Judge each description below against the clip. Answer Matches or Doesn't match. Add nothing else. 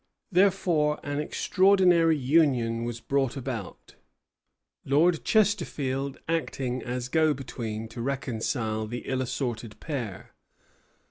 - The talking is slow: Matches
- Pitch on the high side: Doesn't match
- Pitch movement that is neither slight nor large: Matches